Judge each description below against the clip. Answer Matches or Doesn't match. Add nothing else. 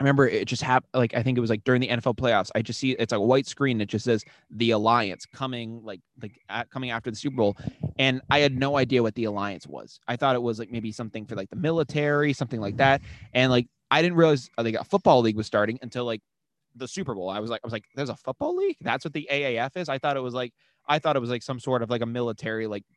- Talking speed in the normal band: Doesn't match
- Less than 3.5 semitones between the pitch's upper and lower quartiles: Matches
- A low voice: Matches